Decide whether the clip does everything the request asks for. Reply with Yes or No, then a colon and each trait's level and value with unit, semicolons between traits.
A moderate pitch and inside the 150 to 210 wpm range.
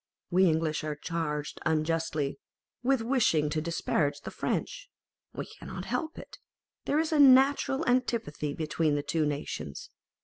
No: medium, 165 Hz; average, 140 wpm